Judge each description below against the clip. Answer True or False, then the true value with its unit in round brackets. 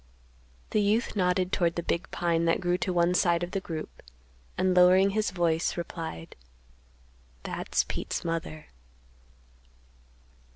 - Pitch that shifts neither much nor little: False (1.7 semitones)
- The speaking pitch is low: False (175 Hz)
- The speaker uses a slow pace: True (130 wpm)